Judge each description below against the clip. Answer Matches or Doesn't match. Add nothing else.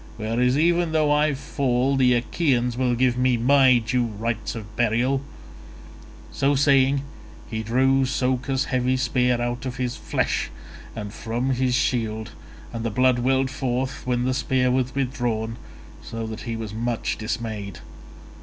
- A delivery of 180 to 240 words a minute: Doesn't match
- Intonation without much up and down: Matches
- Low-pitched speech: Matches